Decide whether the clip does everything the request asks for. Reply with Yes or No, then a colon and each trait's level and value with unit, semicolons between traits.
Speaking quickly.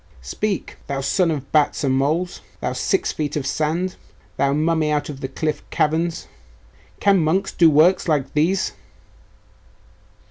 No: average, 145 wpm